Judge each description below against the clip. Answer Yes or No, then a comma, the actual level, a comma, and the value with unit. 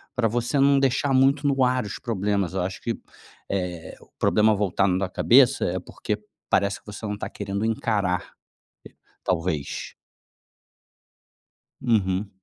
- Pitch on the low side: Yes, low, 105 Hz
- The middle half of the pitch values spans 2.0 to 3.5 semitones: No, average, 4.4 semitones